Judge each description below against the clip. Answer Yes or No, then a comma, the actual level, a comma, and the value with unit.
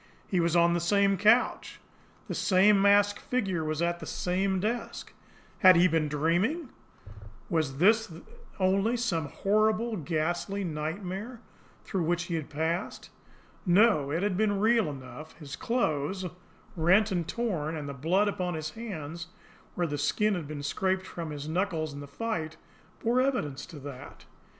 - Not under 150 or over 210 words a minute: Yes, average, 160 wpm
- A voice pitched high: No, medium, 180 Hz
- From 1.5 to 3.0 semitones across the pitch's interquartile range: No, average, 4.6 semitones